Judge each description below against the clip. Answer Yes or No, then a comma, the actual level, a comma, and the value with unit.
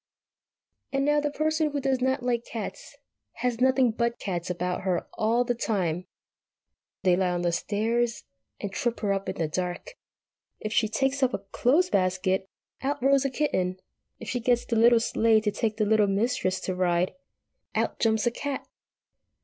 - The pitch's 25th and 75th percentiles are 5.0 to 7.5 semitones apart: Yes, average, 5.3 semitones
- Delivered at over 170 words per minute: Yes, average, 180 wpm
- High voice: Yes, high, 225 Hz